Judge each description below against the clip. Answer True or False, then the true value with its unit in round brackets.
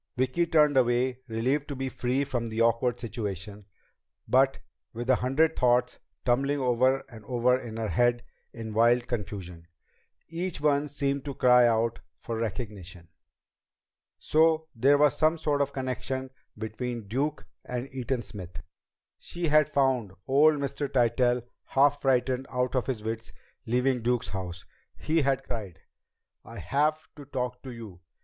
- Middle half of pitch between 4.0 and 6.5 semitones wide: False (3.2 semitones)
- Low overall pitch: True (125 Hz)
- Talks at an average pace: True (150 wpm)